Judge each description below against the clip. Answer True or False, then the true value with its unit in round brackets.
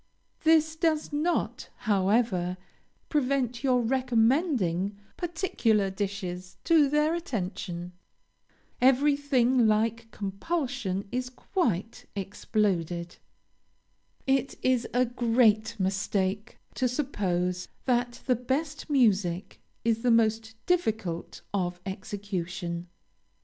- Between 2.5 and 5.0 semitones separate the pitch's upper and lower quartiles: False (5.6 semitones)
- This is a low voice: False (225 Hz)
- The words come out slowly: True (90 wpm)